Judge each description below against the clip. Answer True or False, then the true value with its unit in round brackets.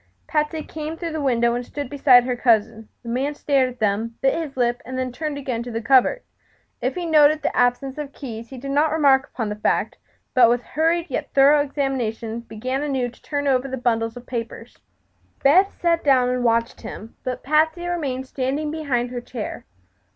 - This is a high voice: True (260 Hz)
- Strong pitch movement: False (3.6 semitones)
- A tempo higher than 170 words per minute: True (200 wpm)